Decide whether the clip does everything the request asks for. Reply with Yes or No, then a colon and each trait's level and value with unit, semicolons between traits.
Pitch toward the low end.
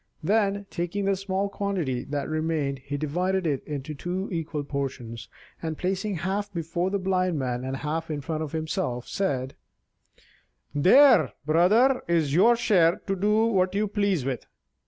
No: medium, 170 Hz